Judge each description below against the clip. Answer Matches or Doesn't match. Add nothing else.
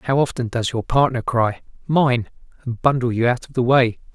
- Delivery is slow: Doesn't match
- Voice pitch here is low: Matches